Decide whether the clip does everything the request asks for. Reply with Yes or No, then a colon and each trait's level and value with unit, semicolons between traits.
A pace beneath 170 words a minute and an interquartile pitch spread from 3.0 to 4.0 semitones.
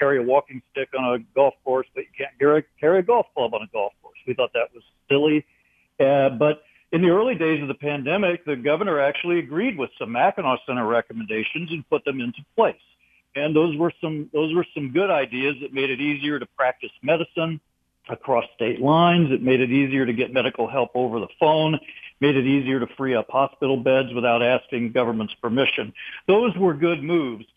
No: fast, 205 wpm; average, 3.5 semitones